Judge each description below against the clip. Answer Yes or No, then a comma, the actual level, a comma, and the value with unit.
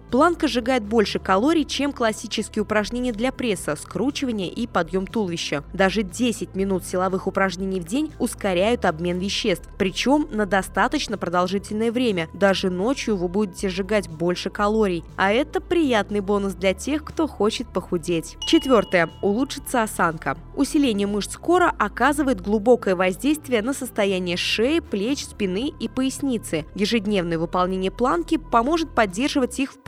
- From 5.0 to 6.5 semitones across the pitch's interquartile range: Yes, wide, 5.5 semitones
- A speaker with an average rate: Yes, average, 135 wpm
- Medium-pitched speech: No, high, 210 Hz